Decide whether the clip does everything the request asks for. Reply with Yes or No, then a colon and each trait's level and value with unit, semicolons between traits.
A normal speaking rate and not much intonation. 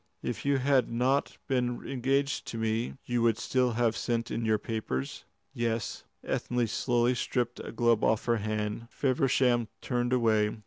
Yes: average, 160 wpm; narrow, 1.9 semitones